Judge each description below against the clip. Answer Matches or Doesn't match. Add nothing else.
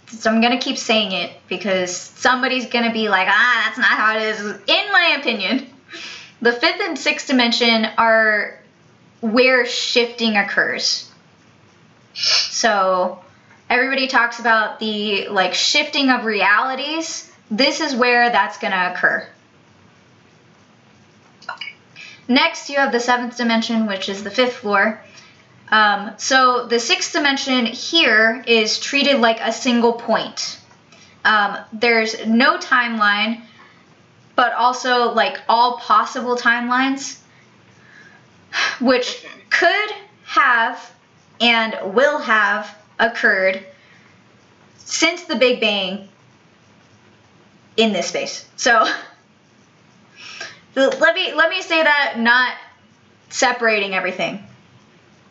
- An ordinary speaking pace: Doesn't match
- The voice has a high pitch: Matches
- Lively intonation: Doesn't match